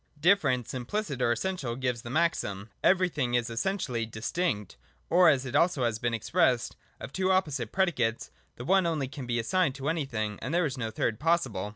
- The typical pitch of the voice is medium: No, low, 130 Hz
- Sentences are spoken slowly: No, average, 185 wpm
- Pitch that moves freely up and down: Yes, wide, 6.4 semitones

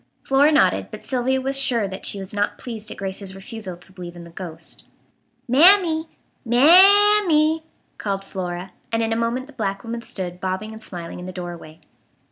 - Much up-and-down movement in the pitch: Yes, wide, 6.4 semitones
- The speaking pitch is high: Yes, high, 220 Hz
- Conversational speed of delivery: Yes, average, 195 wpm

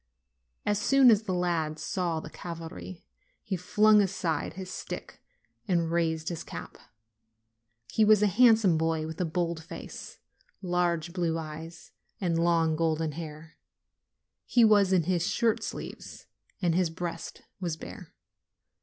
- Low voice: No, medium, 170 Hz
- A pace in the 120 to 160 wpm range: Yes, average, 140 wpm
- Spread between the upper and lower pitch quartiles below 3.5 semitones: Yes, average, 2.8 semitones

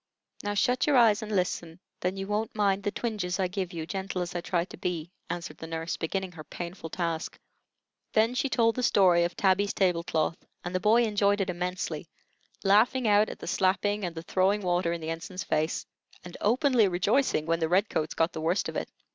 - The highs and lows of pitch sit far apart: No, average, 3.2 semitones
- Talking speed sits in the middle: No, fast, 215 wpm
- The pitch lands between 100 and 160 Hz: No, medium, 185 Hz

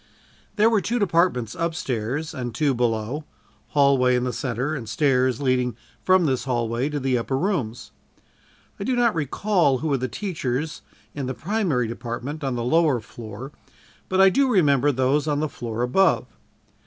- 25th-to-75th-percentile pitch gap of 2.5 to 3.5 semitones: No, average, 4.9 semitones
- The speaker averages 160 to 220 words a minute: Yes, average, 170 wpm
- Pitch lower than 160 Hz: Yes, low, 135 Hz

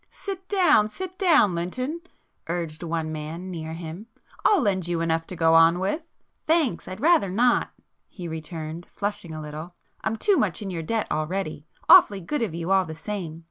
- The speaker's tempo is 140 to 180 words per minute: No, average, 190 wpm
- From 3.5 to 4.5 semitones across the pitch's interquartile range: No, average, 5.1 semitones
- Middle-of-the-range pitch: Yes, medium, 180 Hz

